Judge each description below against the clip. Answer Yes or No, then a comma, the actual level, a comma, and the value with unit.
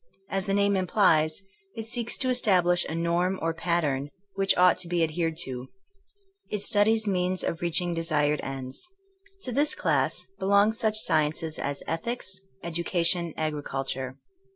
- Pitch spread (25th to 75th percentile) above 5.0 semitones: No, average, 4.1 semitones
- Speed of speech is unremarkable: Yes, average, 150 wpm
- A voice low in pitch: No, medium, 175 Hz